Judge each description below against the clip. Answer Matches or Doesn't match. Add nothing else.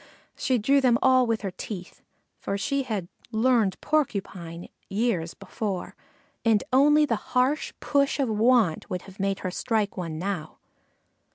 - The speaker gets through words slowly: Doesn't match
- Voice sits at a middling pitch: Doesn't match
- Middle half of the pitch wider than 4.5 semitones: Matches